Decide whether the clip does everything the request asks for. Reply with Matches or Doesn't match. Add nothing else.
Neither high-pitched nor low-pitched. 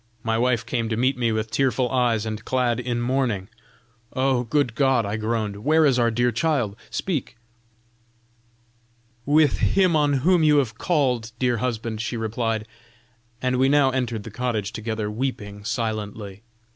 Doesn't match